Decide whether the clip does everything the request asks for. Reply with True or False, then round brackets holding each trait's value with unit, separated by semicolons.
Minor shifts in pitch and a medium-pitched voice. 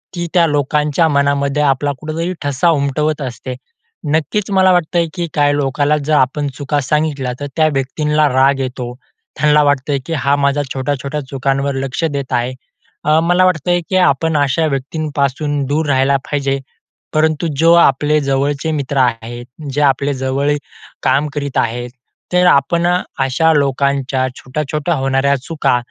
True (2.2 semitones; 145 Hz)